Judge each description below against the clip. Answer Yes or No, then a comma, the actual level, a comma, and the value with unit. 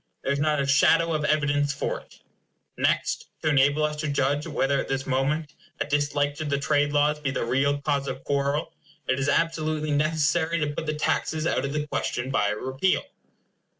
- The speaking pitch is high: No, medium, 145 Hz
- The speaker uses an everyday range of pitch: No, narrow, 1.6 semitones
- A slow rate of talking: No, average, 200 wpm